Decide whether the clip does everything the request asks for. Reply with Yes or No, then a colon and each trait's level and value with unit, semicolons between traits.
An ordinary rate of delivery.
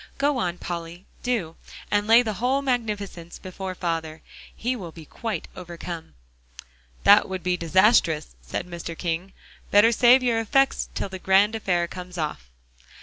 Yes: average, 150 wpm